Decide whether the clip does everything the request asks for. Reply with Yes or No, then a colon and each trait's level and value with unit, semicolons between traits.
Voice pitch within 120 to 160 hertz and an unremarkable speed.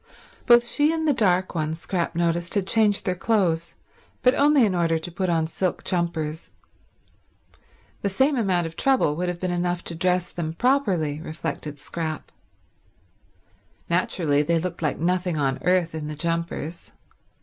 No: medium, 175 Hz; average, 160 wpm